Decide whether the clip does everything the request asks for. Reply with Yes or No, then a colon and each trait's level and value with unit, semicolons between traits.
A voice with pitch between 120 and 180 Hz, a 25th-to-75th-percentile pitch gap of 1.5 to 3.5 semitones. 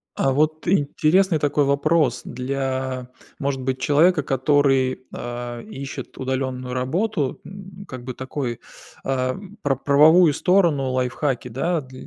Yes: low, 135 Hz; average, 3.0 semitones